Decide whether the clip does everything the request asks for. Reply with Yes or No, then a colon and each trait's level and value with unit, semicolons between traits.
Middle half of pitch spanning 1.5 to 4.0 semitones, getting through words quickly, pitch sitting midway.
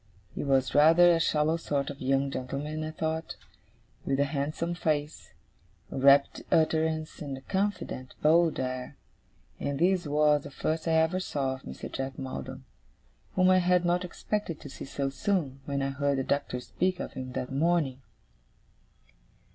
No: average, 3.4 semitones; average, 165 wpm; medium, 150 Hz